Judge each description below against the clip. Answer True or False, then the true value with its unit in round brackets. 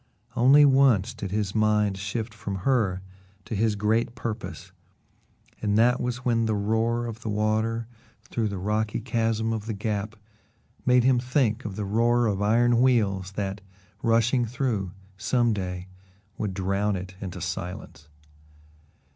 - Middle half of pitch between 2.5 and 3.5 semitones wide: True (2.8 semitones)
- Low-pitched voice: True (110 Hz)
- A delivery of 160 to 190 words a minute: False (145 wpm)